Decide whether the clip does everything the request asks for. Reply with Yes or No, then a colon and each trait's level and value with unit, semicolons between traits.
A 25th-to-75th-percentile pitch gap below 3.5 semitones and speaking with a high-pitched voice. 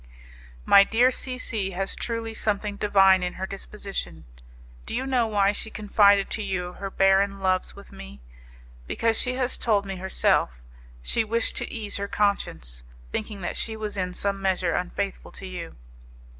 Yes: narrow, 2.4 semitones; high, 200 Hz